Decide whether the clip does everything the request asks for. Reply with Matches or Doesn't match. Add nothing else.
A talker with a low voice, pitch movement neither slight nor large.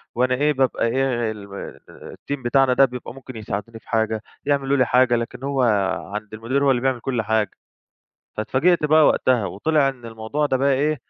Matches